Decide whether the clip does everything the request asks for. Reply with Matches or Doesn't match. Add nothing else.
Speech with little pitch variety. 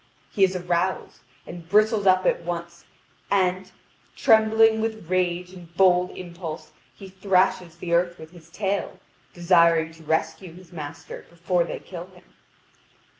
Matches